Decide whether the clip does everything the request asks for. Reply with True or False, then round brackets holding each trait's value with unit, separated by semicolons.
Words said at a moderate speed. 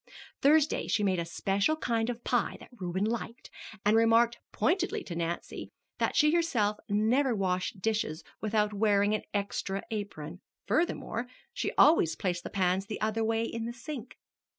True (160 wpm)